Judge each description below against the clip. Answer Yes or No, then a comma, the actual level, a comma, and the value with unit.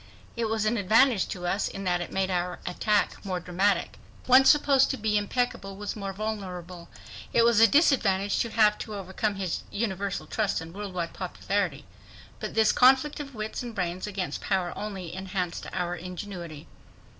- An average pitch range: Yes, average, 3.3 semitones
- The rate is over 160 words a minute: Yes, average, 175 wpm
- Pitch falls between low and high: No, high, 200 Hz